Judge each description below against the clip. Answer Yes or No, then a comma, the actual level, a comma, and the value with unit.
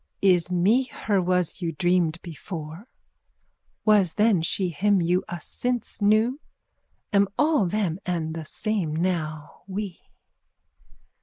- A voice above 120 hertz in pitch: Yes, medium, 185 Hz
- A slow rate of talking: Yes, slow, 130 wpm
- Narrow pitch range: No, average, 3.9 semitones